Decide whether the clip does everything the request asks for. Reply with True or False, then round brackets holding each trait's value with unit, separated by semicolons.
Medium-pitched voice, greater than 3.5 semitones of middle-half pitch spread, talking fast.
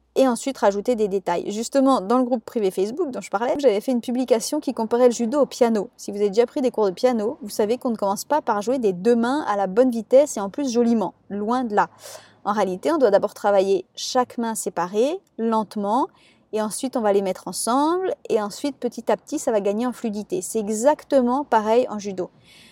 False (230 Hz; 3.9 semitones; 230 wpm)